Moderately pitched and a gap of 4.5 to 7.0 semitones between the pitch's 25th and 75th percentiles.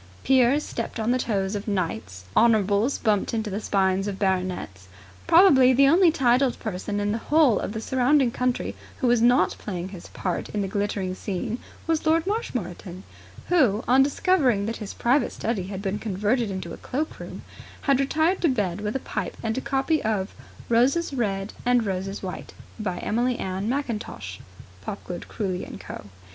No: high, 220 Hz; average, 5.1 semitones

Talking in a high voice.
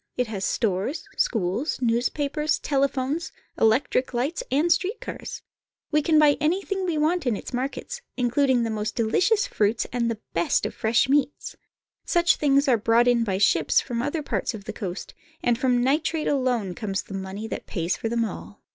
Yes: very high, 250 Hz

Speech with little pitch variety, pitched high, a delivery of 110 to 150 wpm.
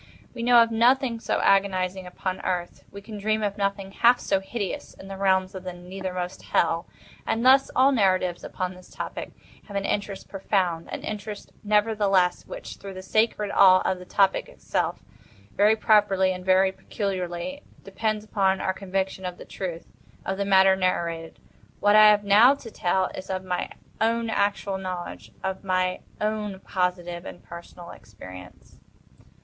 No: narrow, 2.3 semitones; high, 195 Hz; average, 160 wpm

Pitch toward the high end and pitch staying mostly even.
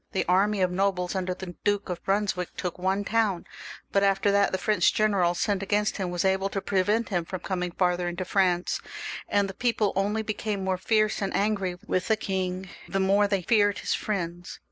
Yes: high, 195 Hz; narrow, 2.1 semitones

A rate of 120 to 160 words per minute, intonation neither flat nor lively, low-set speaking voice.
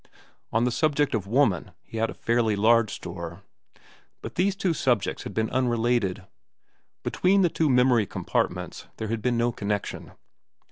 Yes: average, 155 wpm; average, 3.5 semitones; low, 115 Hz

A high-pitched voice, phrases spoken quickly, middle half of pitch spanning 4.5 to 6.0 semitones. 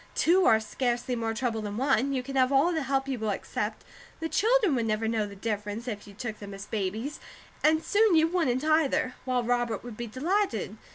Yes: high, 245 Hz; fast, 215 wpm; average, 5.1 semitones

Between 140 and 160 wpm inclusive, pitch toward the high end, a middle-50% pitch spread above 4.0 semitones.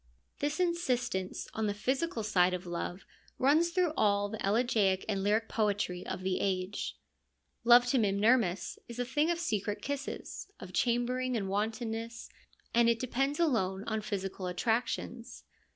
Yes: average, 150 wpm; high, 225 Hz; average, 4.4 semitones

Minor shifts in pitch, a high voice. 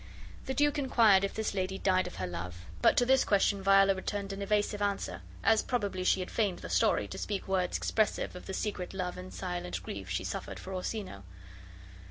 Yes: narrow, 2.3 semitones; high, 195 Hz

